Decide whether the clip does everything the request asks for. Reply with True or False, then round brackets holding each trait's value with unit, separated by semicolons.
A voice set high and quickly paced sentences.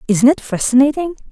False (265 Hz; 135 wpm)